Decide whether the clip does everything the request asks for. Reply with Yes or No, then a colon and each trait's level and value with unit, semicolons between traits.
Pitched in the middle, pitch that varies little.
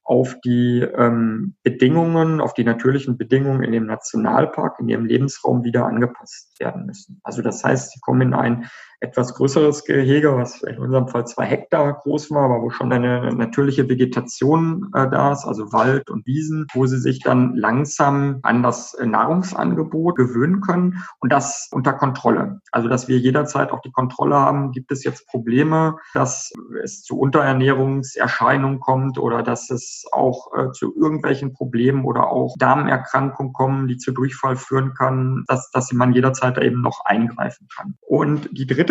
No: low, 130 Hz; narrow, 2.3 semitones